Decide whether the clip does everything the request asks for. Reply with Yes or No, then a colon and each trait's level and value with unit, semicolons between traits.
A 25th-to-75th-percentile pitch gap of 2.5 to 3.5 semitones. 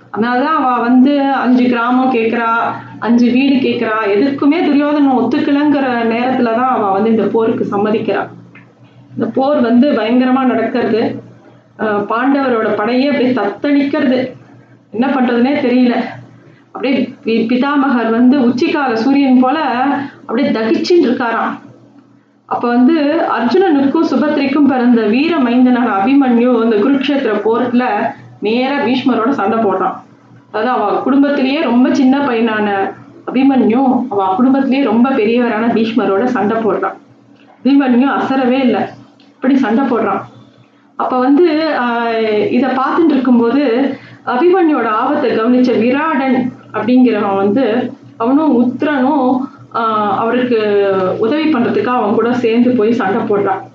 Yes: average, 3.1 semitones